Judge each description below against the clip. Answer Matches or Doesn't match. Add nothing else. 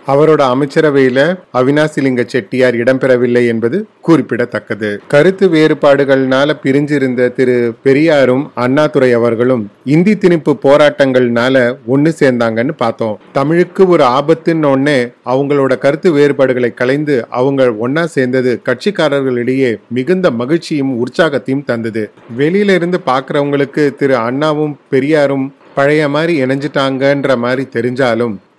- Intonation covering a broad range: Doesn't match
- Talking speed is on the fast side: Doesn't match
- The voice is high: Doesn't match